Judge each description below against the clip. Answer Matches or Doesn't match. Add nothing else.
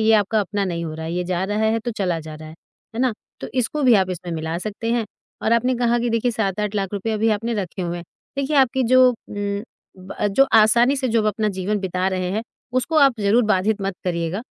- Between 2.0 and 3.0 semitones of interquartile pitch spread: Doesn't match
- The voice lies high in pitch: Matches